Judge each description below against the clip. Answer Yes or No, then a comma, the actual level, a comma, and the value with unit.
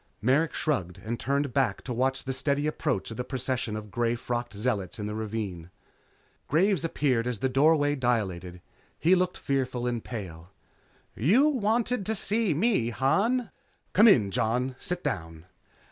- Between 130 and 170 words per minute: Yes, average, 160 wpm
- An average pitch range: No, wide, 6.2 semitones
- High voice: No, low, 130 Hz